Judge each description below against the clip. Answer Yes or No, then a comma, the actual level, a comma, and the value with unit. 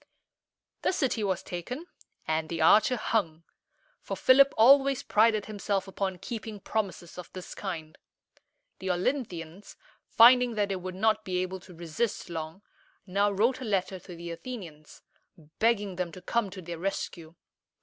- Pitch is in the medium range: No, high, 195 Hz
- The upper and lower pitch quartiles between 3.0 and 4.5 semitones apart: Yes, average, 4.2 semitones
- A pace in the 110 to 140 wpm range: No, average, 150 wpm